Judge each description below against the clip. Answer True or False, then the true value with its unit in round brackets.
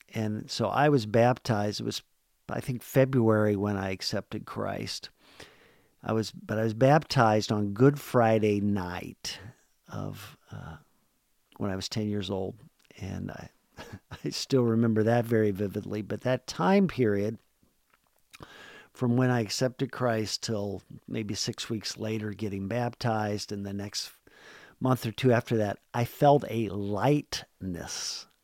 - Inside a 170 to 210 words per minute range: False (145 wpm)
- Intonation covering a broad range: False (3.3 semitones)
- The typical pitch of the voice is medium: False (110 Hz)